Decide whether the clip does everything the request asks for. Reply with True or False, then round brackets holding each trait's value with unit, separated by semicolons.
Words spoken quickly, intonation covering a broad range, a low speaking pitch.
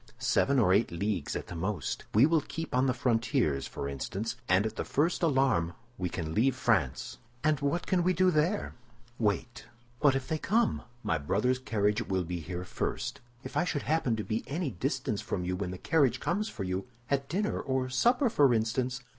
False (195 wpm; 7.6 semitones; 120 Hz)